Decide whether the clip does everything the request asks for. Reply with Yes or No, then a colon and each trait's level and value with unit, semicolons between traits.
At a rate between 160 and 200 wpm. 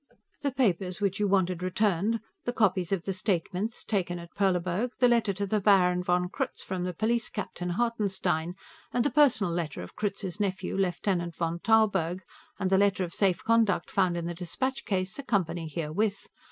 Yes: average, 180 wpm